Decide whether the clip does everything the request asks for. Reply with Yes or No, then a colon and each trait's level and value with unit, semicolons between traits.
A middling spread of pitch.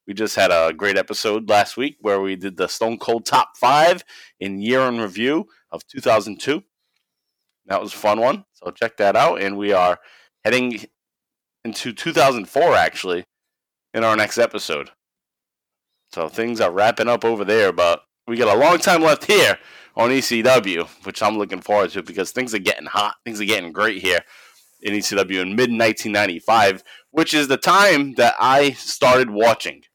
Yes: average, 3.3 semitones